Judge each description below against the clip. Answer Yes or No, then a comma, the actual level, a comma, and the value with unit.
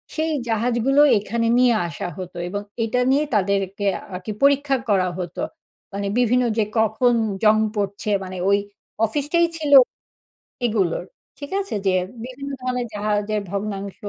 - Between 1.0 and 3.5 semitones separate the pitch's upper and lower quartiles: No, average, 4.1 semitones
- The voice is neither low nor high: No, high, 220 Hz